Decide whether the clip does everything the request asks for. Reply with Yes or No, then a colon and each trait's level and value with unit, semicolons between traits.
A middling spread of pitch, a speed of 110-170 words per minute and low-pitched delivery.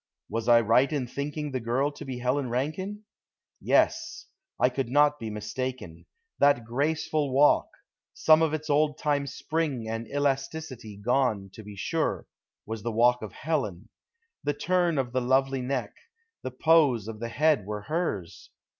Yes: average, 4.2 semitones; average, 160 wpm; low, 130 Hz